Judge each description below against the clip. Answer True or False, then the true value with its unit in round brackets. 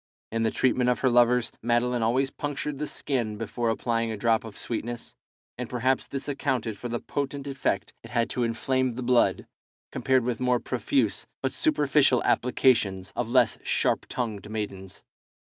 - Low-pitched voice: True (120 Hz)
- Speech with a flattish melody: True (2.3 semitones)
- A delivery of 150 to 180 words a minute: True (165 wpm)